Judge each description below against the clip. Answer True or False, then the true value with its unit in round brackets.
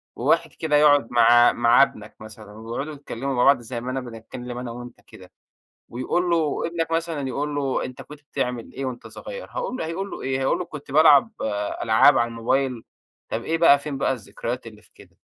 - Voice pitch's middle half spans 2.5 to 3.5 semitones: False (4.0 semitones)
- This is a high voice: False (135 Hz)